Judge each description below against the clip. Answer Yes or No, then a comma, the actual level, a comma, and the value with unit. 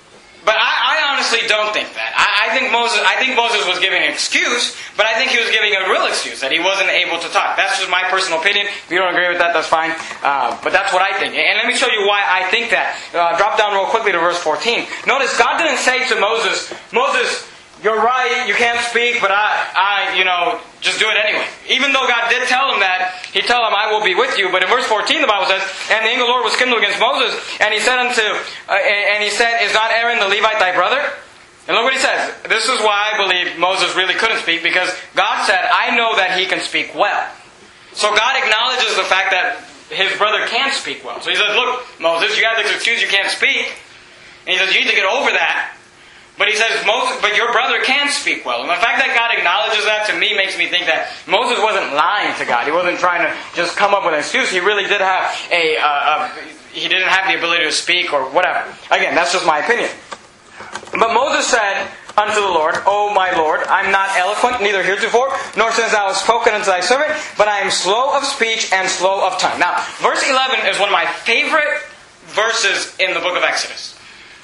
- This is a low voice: No, high, 205 Hz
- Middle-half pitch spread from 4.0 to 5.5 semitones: Yes, average, 4.3 semitones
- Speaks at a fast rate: Yes, fast, 240 wpm